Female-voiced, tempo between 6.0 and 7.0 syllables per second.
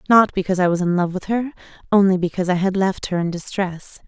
Yes: female; 6.4 syllables/s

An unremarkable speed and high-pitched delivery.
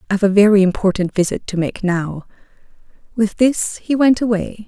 Yes: average, 165 wpm; high, 205 Hz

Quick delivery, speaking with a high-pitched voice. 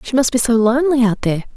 Yes: fast, 270 wpm; high, 245 Hz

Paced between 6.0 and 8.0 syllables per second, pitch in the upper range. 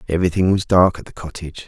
No: 7.4 syllables/s; very low, 90 Hz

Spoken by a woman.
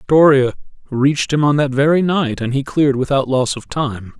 No: male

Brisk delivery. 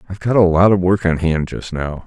Yes: fast, 290 wpm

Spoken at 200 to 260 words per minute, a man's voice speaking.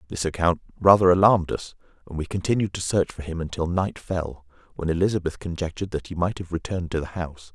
Yes: fast, 205 wpm; male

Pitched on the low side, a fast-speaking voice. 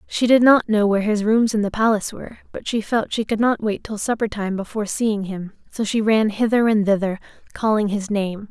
No: high, 215 Hz; fast, 235 wpm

